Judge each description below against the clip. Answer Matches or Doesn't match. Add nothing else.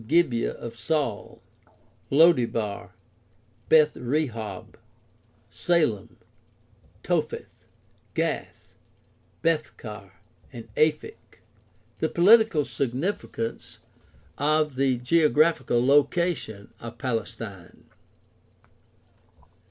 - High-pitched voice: Doesn't match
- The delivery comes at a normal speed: Doesn't match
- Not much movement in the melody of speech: Doesn't match